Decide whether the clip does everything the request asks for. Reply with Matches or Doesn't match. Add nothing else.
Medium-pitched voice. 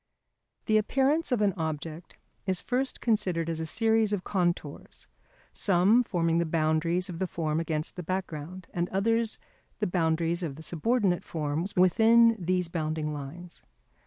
Matches